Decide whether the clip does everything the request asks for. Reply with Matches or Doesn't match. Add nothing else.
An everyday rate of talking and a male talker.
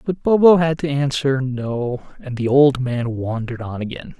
Matches